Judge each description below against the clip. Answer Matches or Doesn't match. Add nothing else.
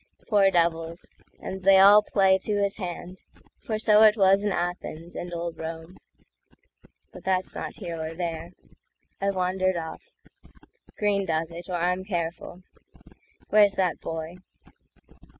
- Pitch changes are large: Doesn't match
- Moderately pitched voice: Matches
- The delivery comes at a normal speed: Doesn't match